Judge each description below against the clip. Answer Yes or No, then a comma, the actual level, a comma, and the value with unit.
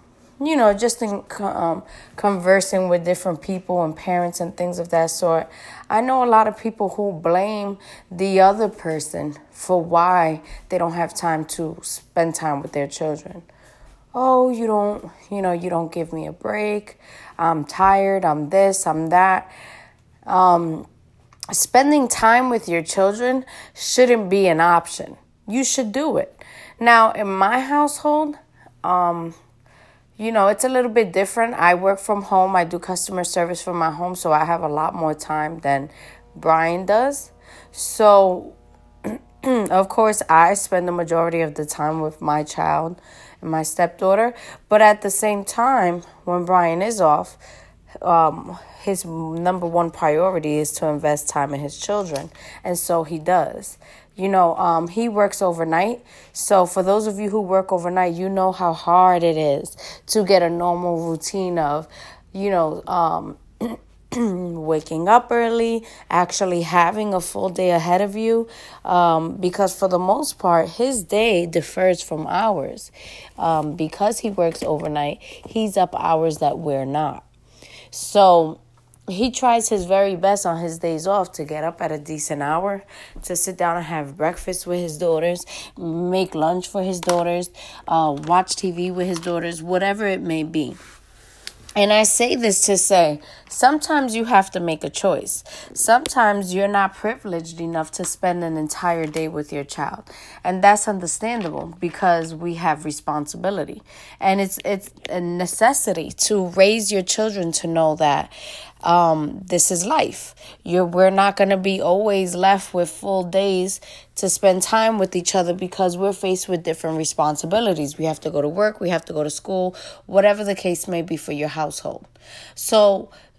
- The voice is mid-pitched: Yes, medium, 180 Hz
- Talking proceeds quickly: No, average, 165 wpm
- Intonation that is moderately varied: Yes, average, 3.5 semitones